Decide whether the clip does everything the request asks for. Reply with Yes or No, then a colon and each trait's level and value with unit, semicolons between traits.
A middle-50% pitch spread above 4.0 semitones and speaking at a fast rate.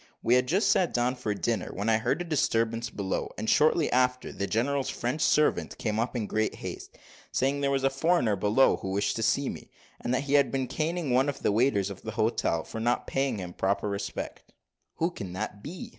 Yes: average, 4.4 semitones; fast, 220 wpm